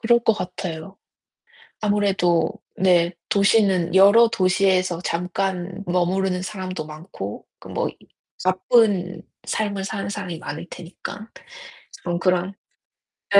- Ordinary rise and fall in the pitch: No, narrow, 2.2 semitones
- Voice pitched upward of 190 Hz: No, medium, 185 Hz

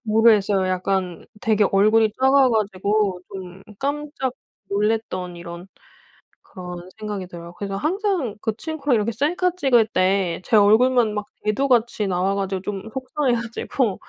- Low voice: No, high, 210 Hz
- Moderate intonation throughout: Yes, average, 4.5 semitones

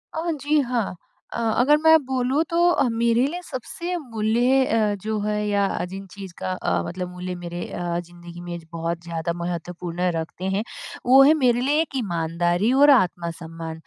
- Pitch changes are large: Yes, wide, 6.9 semitones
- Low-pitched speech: No, high, 205 Hz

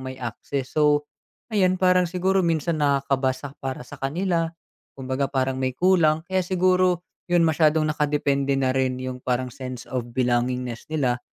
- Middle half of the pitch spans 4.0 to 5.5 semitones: Yes, average, 4.6 semitones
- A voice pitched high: No, medium, 140 Hz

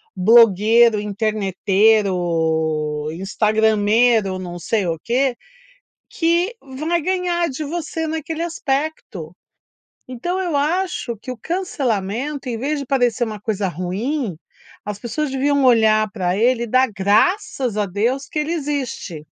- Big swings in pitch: Yes, wide, 6.4 semitones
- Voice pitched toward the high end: Yes, high, 235 Hz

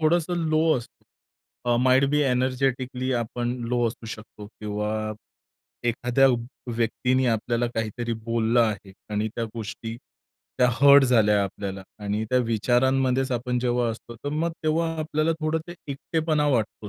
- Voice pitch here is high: No, low, 120 Hz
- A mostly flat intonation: No, average, 3.0 semitones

